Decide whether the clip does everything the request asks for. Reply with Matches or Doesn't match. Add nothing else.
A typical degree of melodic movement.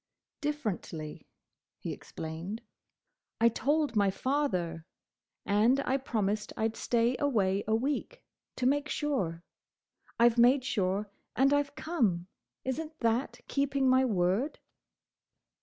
Doesn't match